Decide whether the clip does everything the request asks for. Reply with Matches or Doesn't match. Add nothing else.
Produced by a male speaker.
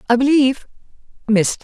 Doesn't match